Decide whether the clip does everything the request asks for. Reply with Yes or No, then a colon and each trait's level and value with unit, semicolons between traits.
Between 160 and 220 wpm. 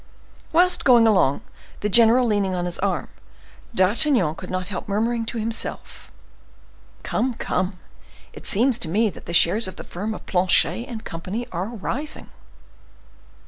No: average, 145 wpm